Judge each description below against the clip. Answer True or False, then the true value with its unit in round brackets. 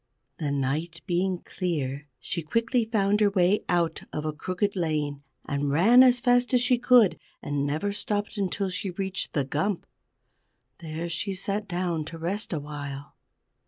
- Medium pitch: True (175 Hz)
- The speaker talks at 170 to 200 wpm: False (160 wpm)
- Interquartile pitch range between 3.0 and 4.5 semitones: False (5.2 semitones)